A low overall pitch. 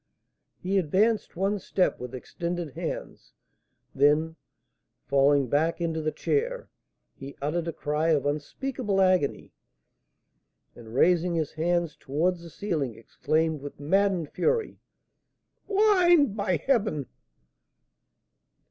No: medium, 170 Hz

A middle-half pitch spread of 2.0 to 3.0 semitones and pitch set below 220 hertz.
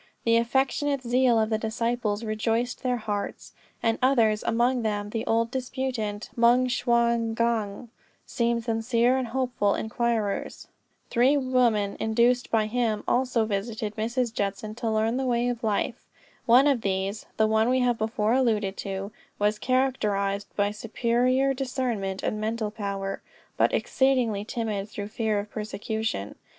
No: narrow, 2.6 semitones; high, 230 Hz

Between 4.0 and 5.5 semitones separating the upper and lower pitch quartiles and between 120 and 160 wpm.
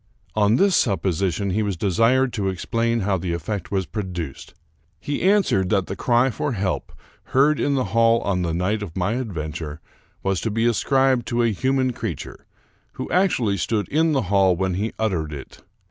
No: average, 4.7 semitones; average, 180 wpm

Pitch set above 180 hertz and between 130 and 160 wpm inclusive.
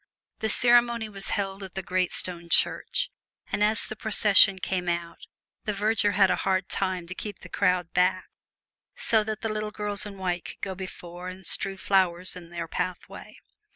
No: high, 190 Hz; average, 185 wpm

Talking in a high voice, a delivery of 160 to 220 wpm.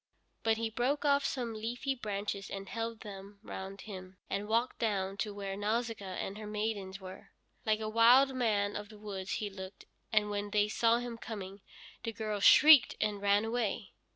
Yes: high, 210 Hz; average, 180 wpm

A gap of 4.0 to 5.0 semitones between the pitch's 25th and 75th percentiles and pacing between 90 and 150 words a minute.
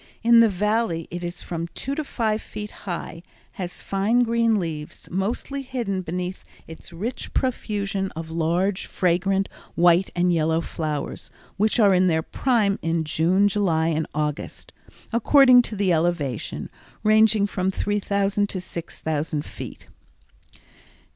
Yes: average, 4.3 semitones; slow, 135 wpm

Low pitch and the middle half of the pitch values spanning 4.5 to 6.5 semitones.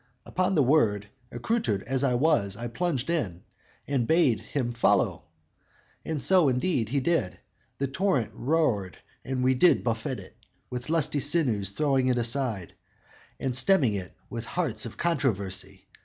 Yes: low, 130 Hz; average, 5.2 semitones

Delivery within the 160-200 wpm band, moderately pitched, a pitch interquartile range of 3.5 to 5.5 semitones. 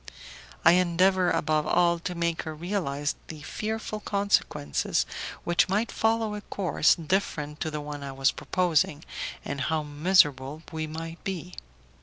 No: average, 145 wpm; medium, 165 Hz; average, 3.9 semitones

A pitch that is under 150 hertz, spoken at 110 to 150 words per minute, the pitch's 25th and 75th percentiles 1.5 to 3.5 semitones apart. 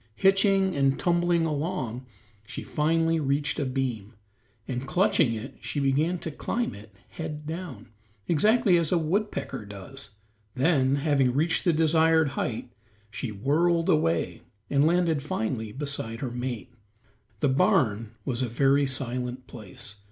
No: medium, 140 Hz; slow, 135 wpm; average, 4.8 semitones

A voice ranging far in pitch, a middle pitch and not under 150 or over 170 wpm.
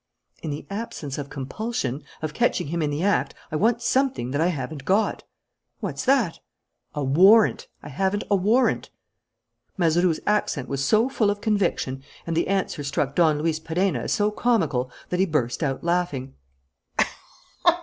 Yes: wide, 6.1 semitones; medium, 170 Hz; average, 160 wpm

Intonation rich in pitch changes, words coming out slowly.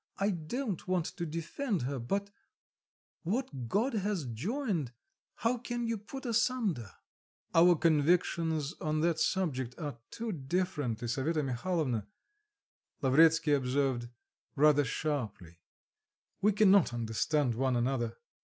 Yes: wide, 6.9 semitones; slow, 115 wpm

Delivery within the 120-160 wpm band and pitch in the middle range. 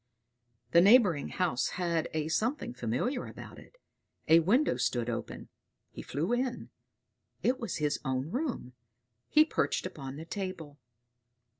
Yes: slow, 135 wpm; medium, 165 Hz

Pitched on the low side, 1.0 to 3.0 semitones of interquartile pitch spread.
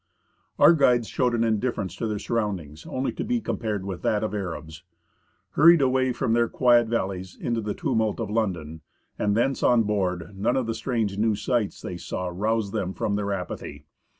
No: low, 110 Hz; average, 3.6 semitones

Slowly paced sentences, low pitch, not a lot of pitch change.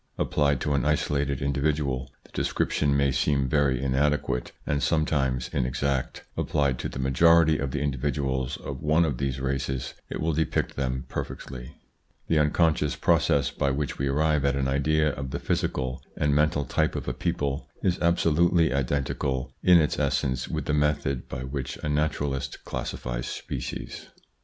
No: average, 160 wpm; very low, 70 Hz; narrow, 2.2 semitones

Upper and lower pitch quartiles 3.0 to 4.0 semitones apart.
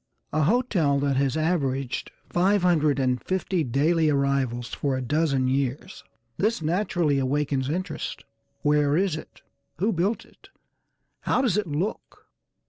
No: average, 4.6 semitones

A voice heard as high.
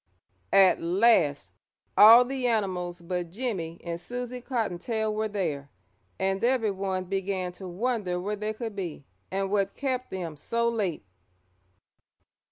Yes: high, 195 Hz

